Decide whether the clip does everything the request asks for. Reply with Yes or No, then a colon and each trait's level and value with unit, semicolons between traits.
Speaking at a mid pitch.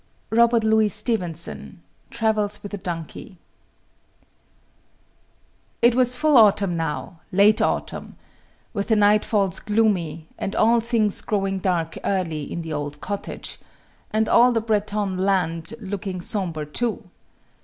No: high, 200 Hz